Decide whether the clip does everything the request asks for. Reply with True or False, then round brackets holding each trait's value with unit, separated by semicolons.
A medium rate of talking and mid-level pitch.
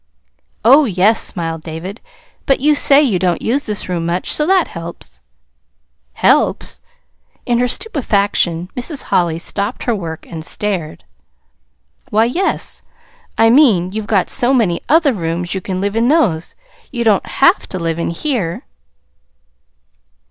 False (145 wpm; 205 Hz)